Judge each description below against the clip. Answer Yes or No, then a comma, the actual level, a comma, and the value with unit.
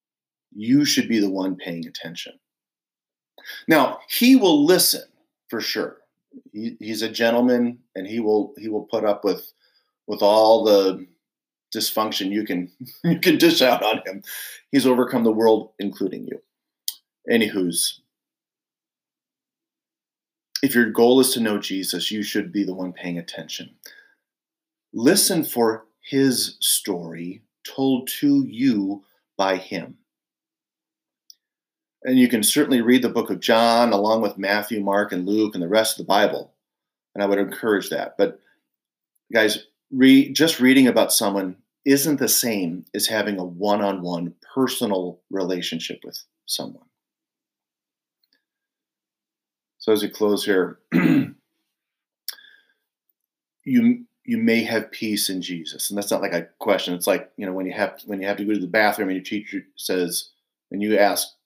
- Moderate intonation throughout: No, wide, 5.9 semitones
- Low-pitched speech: Yes, low, 110 Hz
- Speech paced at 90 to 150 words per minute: Yes, average, 145 wpm